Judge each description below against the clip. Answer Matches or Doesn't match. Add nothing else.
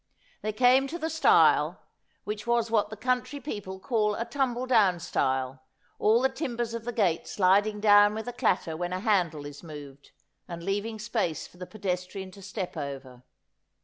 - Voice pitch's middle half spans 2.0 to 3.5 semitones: Doesn't match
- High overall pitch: Matches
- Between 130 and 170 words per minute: Doesn't match